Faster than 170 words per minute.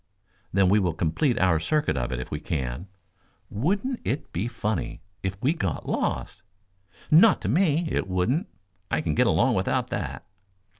No: average, 165 wpm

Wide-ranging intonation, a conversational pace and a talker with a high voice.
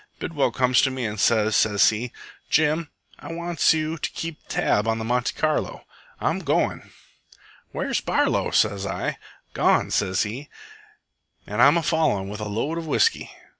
No: wide, 6.6 semitones; average, 165 wpm; low, 125 Hz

